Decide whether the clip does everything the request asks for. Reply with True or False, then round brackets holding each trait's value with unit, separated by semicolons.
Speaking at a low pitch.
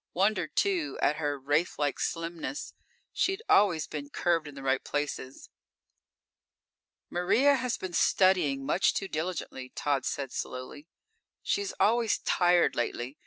False (165 Hz)